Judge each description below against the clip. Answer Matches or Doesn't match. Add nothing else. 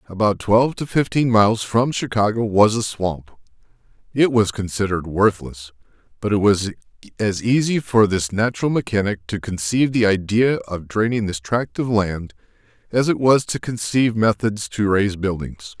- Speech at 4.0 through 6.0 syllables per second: Matches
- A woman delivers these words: Doesn't match